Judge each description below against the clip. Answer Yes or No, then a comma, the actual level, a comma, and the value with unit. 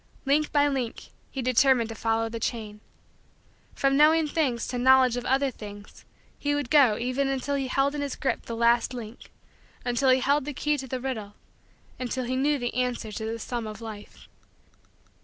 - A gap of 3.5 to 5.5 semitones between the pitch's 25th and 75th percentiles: No, average, 3.1 semitones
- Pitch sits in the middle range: No, very high, 255 Hz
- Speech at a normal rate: Yes, average, 190 wpm